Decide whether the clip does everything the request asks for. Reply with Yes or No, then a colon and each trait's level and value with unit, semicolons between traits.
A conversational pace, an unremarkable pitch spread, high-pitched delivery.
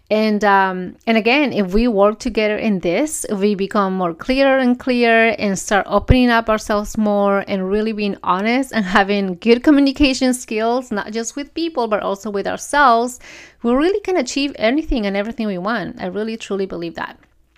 Yes: average, 180 wpm; average, 3.8 semitones; high, 220 Hz